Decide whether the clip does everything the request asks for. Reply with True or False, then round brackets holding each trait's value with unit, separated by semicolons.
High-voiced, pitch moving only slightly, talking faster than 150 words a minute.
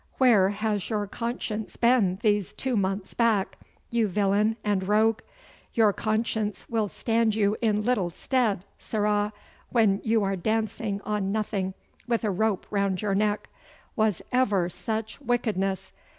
False (210 Hz; 2.1 semitones; 140 wpm)